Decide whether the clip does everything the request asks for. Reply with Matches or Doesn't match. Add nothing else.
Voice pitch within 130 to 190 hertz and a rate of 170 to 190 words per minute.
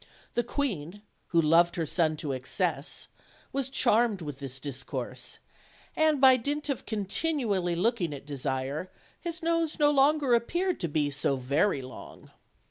Doesn't match